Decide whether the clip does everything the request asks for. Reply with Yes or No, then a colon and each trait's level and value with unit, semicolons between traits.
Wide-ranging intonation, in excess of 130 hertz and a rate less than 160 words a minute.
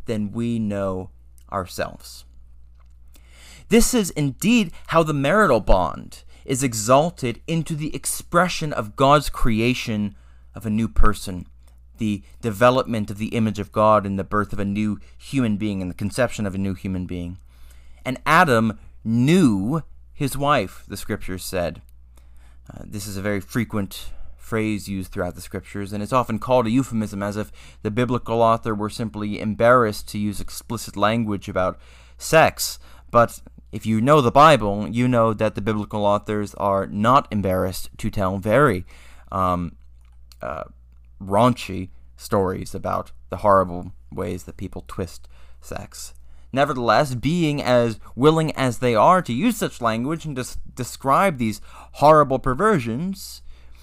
No: wide, 6.1 semitones; low, 105 Hz; average, 150 wpm